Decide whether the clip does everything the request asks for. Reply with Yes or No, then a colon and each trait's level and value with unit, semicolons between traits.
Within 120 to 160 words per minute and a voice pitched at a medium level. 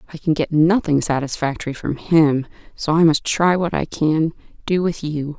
No: average, 190 wpm; medium, 160 Hz